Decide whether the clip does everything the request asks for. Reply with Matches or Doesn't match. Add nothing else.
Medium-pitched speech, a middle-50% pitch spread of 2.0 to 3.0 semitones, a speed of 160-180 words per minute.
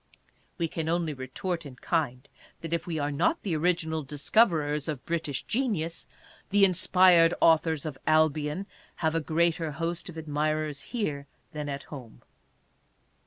Doesn't match